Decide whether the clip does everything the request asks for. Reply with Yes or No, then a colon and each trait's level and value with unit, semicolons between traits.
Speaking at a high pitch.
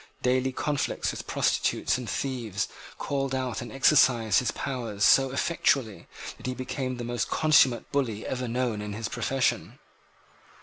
No: low, 125 Hz